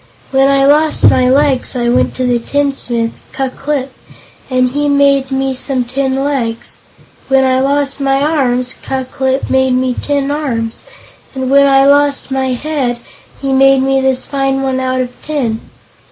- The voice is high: Yes, very high, 270 Hz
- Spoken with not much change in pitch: Yes, narrow, 1.5 semitones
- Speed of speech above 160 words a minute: Yes, average, 170 wpm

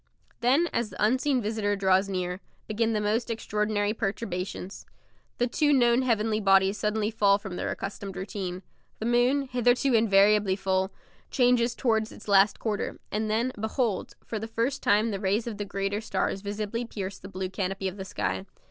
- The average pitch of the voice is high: Yes, high, 210 Hz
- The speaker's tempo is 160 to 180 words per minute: Yes, average, 175 wpm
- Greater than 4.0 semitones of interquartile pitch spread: No, average, 3.0 semitones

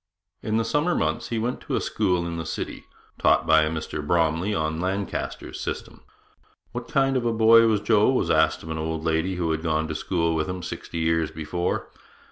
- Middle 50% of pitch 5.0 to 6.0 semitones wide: Yes, wide, 5.5 semitones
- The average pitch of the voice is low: Yes, very low, 85 Hz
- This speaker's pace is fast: Yes, fast, 210 wpm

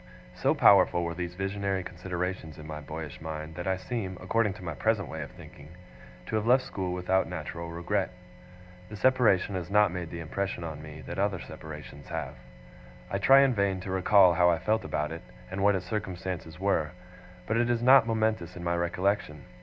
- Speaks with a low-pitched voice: Yes, very low, 90 Hz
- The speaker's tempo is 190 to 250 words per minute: Yes, average, 195 wpm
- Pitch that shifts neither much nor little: Yes, average, 3.4 semitones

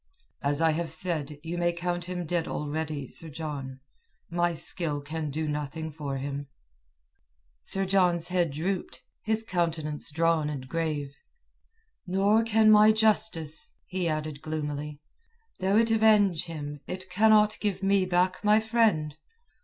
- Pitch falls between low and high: Yes, medium, 165 Hz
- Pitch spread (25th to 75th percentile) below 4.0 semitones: No, average, 4.3 semitones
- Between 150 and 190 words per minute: No, average, 140 wpm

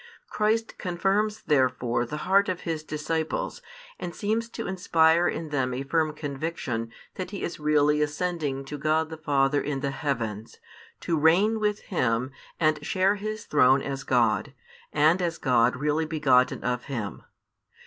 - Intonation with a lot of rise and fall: No, average, 4.5 semitones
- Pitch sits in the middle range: Yes, medium, 155 Hz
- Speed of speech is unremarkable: Yes, average, 155 wpm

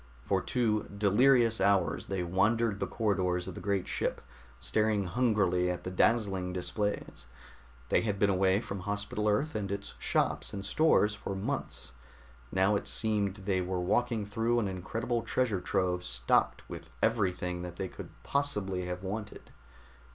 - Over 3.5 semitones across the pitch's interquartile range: No, average, 3.0 semitones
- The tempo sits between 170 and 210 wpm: No, average, 155 wpm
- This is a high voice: No, low, 100 Hz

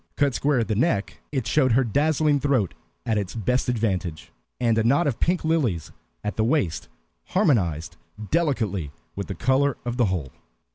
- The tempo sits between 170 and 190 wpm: Yes, average, 175 wpm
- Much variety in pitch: Yes, wide, 6.3 semitones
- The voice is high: No, low, 120 Hz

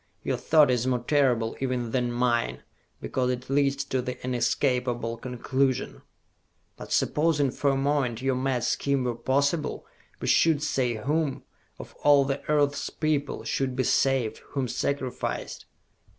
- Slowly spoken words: No, average, 145 wpm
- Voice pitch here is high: No, low, 130 Hz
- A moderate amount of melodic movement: No, narrow, 2.3 semitones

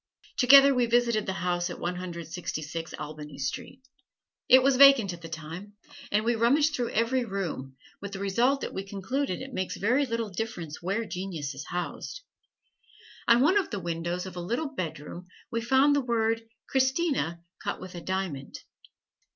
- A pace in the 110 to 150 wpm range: No, average, 175 wpm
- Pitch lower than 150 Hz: No, high, 200 Hz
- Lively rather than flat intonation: Yes, wide, 6.4 semitones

